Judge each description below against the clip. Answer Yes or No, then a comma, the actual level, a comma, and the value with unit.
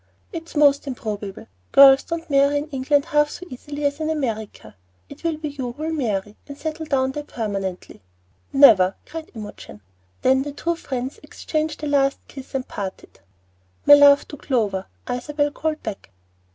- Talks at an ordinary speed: Yes, average, 165 wpm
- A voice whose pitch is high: Yes, very high, 280 Hz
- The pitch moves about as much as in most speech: Yes, average, 3.9 semitones